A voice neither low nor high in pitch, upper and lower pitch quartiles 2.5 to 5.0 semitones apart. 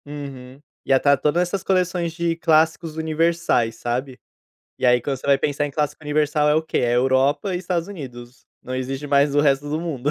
Yes: medium, 145 Hz; average, 3.6 semitones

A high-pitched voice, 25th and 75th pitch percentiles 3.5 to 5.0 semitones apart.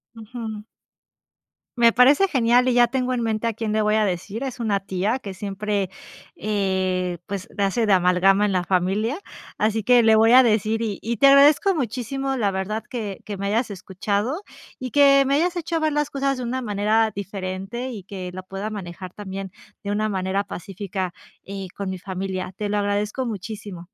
Yes: high, 210 Hz; average, 3.8 semitones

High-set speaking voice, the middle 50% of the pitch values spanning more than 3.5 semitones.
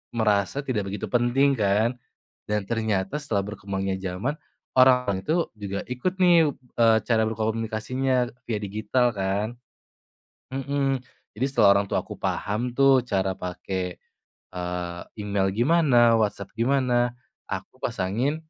No: low, 110 Hz; average, 4.4 semitones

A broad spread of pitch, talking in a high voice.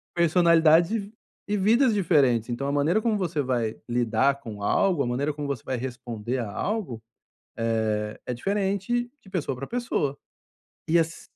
No: wide, 7.6 semitones; medium, 145 Hz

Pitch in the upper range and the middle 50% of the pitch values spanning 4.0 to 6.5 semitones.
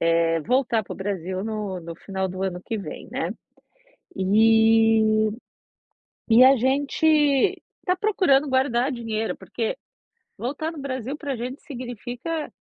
Yes: high, 235 Hz; average, 4.5 semitones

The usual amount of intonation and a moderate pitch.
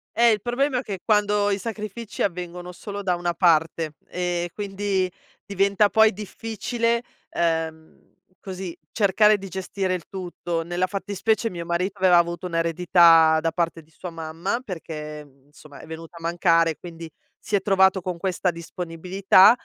Yes: average, 3.3 semitones; medium, 180 Hz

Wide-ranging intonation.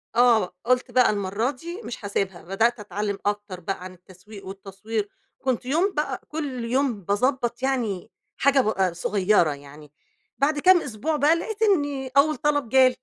Yes: wide, 6.0 semitones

